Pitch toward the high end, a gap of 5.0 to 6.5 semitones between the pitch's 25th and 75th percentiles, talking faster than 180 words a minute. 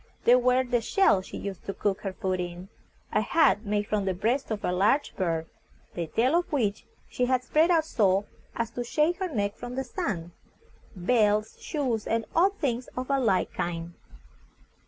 Yes: high, 225 Hz; average, 5.3 semitones; average, 190 wpm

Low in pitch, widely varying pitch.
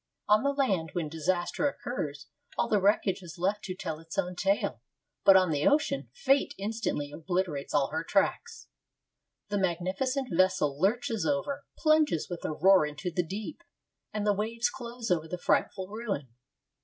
No: high, 190 Hz; wide, 5.9 semitones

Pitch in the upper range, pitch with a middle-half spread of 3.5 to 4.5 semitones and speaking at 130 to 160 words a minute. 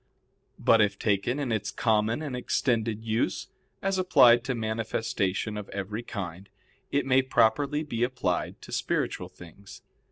No: low, 115 Hz; average, 3.9 semitones; average, 140 wpm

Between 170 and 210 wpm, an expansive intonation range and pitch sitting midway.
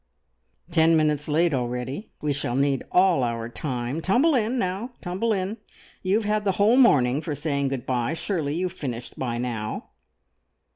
Yes: average, 175 wpm; wide, 6.9 semitones; medium, 155 Hz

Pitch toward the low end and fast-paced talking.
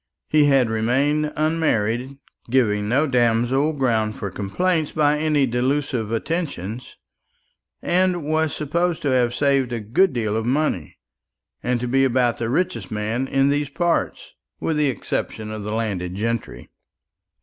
No: low, 130 Hz; average, 145 wpm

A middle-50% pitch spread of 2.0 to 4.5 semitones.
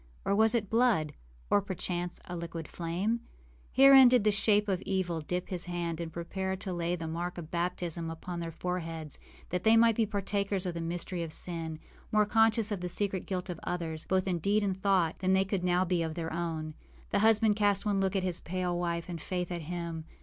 Yes: average, 3.0 semitones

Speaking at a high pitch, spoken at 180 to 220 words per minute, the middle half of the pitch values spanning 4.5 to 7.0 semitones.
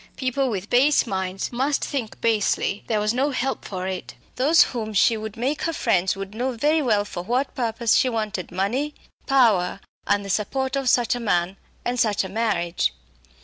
Yes: high, 225 Hz; average, 190 wpm; average, 4.8 semitones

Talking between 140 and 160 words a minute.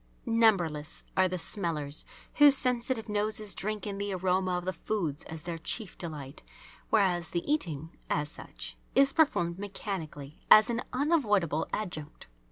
Yes: average, 145 wpm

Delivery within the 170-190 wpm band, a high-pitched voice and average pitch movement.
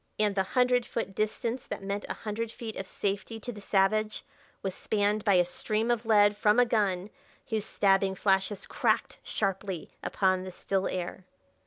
No: average, 175 wpm; high, 205 Hz; narrow, 2.2 semitones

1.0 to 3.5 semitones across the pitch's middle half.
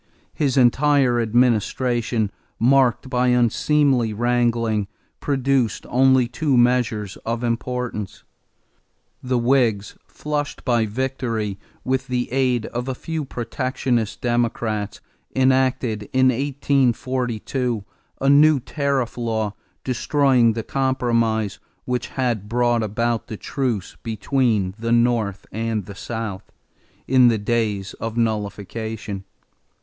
Yes: average, 2.8 semitones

